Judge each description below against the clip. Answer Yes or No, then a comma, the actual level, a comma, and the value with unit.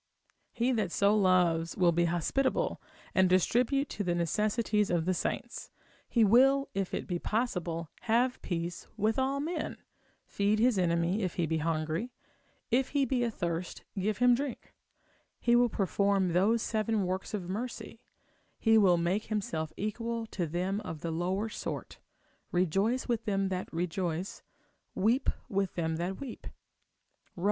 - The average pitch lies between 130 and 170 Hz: No, high, 195 Hz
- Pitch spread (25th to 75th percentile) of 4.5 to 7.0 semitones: Yes, average, 4.9 semitones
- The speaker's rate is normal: Yes, average, 155 wpm